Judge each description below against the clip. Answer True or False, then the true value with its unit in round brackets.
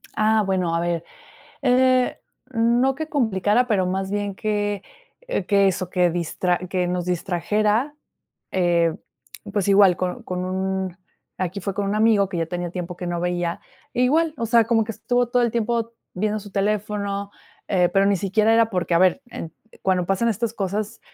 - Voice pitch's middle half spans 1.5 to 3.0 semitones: False (3.7 semitones)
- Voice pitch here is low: False (200 Hz)